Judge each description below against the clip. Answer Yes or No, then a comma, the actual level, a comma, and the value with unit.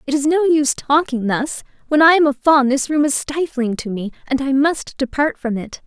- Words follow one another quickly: Yes, fast, 235 wpm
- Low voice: No, very high, 280 Hz